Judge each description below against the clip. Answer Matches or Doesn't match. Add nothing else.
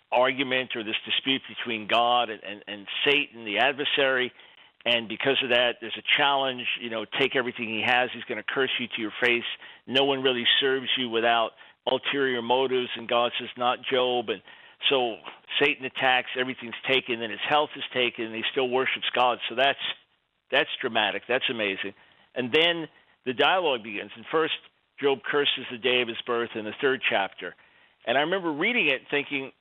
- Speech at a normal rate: Matches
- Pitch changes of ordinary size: Doesn't match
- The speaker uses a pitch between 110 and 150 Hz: Matches